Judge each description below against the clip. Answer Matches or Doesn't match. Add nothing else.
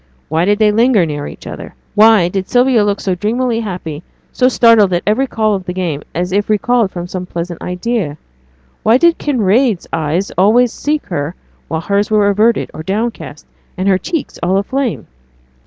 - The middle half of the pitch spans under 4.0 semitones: Doesn't match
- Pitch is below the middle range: Doesn't match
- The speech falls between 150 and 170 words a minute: Doesn't match